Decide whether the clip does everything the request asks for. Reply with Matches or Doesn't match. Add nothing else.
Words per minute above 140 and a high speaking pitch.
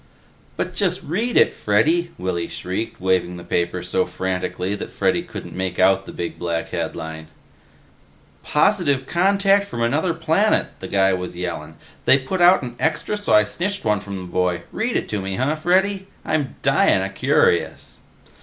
Doesn't match